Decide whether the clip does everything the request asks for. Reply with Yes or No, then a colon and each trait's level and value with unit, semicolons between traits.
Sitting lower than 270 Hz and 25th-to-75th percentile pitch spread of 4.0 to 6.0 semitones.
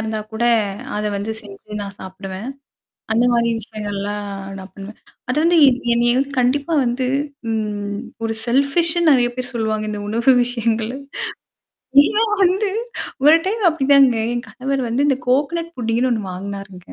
Yes: high, 235 Hz; average, 4.4 semitones